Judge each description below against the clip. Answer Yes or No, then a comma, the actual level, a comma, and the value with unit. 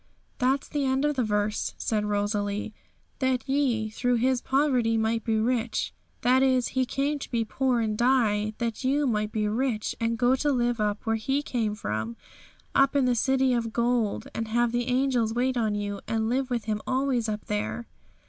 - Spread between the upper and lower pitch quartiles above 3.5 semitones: No, average, 3.2 semitones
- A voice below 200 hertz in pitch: No, high, 235 Hz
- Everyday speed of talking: Yes, average, 190 wpm